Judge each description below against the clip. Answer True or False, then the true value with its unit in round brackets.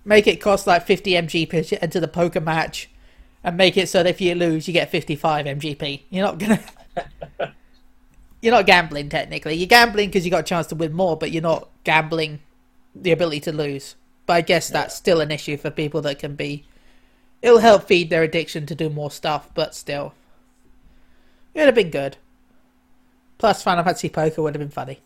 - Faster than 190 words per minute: True (200 wpm)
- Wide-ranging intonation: False (3.1 semitones)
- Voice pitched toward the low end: False (165 Hz)